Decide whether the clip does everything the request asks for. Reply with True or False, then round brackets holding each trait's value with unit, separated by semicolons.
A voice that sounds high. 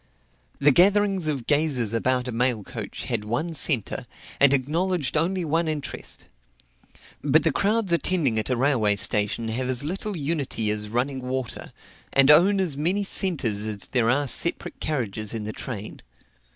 False (135 Hz)